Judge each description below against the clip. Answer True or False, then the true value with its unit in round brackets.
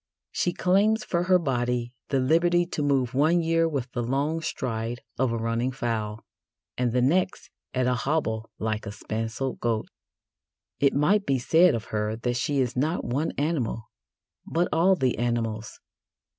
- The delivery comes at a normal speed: True (165 wpm)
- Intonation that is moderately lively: False (5.7 semitones)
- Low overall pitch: True (130 Hz)